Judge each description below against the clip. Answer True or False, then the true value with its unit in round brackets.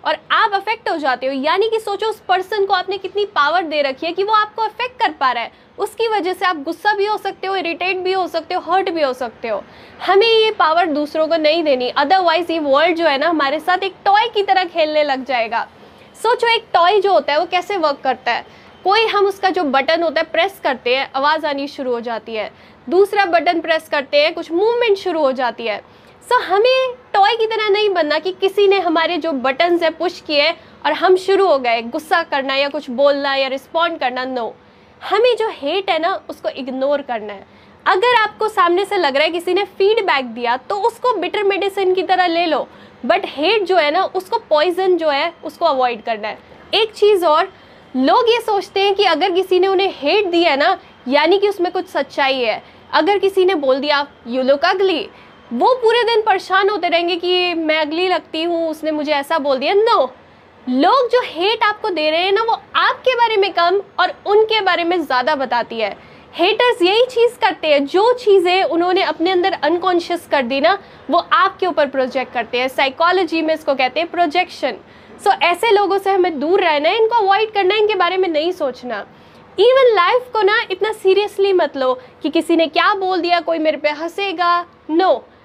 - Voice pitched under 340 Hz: False (350 Hz)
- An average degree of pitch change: True (4.8 semitones)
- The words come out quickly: True (215 wpm)